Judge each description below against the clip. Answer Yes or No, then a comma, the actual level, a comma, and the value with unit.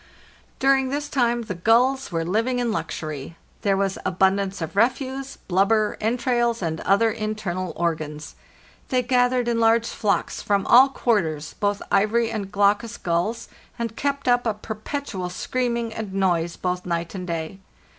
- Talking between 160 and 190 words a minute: No, average, 150 wpm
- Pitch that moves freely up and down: No, average, 4.5 semitones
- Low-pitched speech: No, high, 215 Hz